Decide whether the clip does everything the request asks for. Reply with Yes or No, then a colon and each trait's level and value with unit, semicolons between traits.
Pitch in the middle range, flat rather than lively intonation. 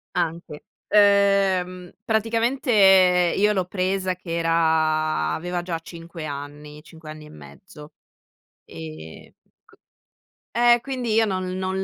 No: medium, 180 Hz; average, 4.1 semitones